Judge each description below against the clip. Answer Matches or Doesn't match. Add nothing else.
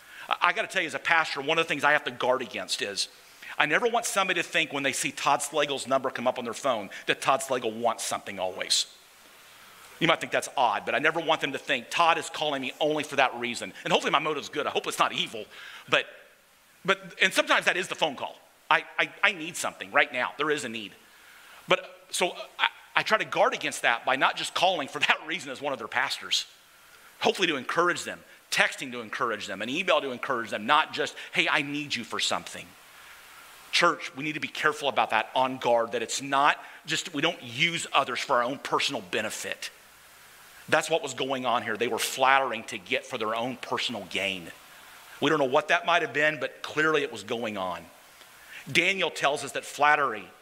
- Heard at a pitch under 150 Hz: Doesn't match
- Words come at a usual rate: Doesn't match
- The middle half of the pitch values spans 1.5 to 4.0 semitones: Doesn't match